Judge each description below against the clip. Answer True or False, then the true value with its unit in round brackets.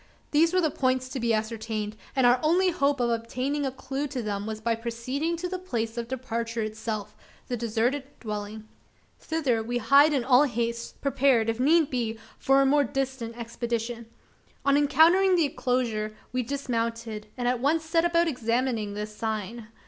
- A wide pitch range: False (3.7 semitones)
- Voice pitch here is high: True (245 Hz)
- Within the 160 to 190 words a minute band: True (175 wpm)